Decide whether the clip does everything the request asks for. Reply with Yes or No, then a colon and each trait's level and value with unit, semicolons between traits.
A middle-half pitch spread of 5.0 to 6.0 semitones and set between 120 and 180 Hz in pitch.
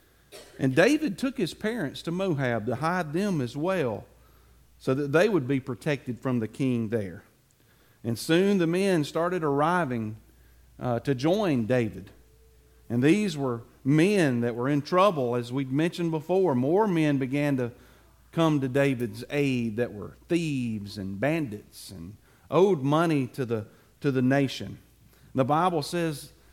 Yes: wide, 5.6 semitones; low, 135 Hz